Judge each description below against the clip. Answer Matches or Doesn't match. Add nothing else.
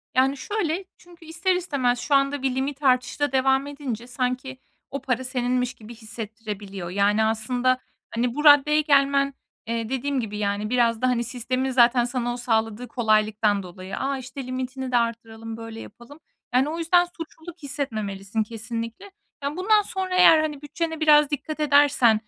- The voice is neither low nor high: Doesn't match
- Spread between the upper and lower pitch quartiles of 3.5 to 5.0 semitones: Matches